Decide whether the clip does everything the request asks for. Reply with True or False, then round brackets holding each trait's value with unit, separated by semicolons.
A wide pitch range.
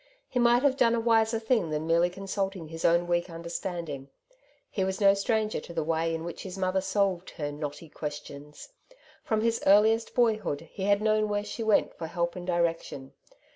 False (4.5 semitones)